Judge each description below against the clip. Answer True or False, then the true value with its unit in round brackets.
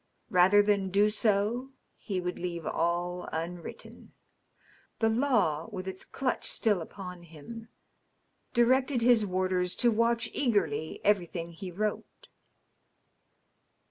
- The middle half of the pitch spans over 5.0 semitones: False (4.3 semitones)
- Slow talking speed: True (110 wpm)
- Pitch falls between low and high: False (195 Hz)